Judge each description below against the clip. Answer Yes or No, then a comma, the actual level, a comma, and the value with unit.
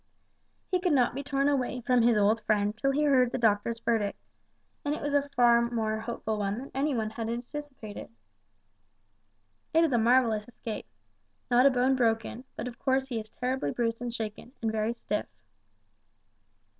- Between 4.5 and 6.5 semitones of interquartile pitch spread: No, average, 3.1 semitones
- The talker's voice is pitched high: Yes, high, 240 Hz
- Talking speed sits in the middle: Yes, average, 175 wpm